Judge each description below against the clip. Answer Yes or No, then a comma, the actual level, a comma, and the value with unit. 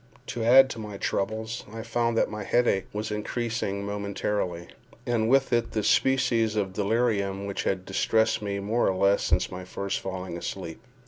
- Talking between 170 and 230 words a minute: Yes, average, 175 wpm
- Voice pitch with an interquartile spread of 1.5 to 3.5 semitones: Yes, average, 2.9 semitones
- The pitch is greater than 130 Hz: No, low, 105 Hz